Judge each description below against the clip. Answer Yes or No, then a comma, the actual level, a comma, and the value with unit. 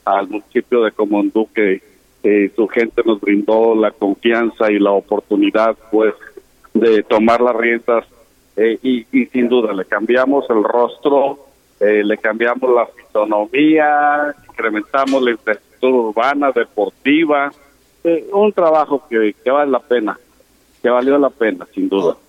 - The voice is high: No, low, 120 Hz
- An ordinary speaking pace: Yes, average, 145 wpm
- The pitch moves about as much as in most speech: Yes, average, 4.1 semitones